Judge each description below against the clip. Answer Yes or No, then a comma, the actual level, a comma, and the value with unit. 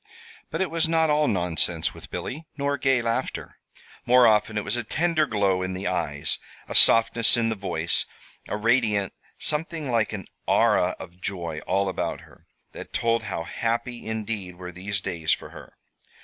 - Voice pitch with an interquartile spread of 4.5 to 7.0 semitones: Yes, average, 5.2 semitones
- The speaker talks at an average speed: Yes, average, 175 wpm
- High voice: No, low, 110 Hz